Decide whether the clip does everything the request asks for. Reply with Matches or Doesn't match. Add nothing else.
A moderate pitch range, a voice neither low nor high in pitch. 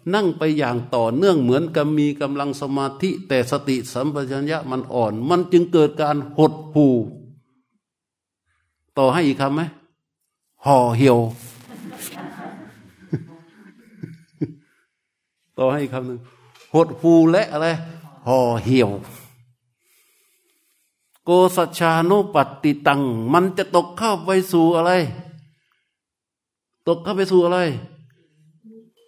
Matches